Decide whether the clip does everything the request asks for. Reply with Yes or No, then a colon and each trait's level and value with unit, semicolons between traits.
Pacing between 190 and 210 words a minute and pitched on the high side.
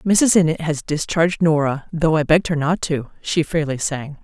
No: average, 200 wpm; medium, 160 Hz